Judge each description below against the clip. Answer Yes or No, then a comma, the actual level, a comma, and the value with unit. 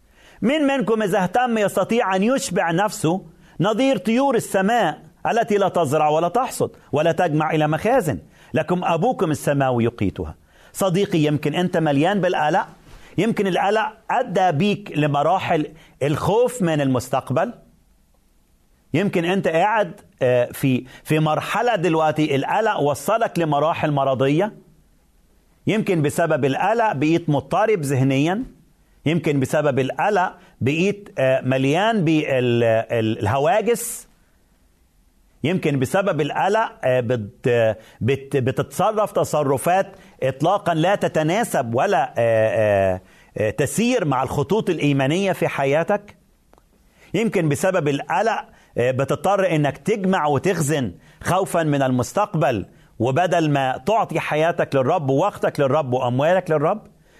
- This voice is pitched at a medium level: Yes, medium, 160 Hz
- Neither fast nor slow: Yes, average, 100 wpm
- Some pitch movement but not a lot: No, wide, 6.0 semitones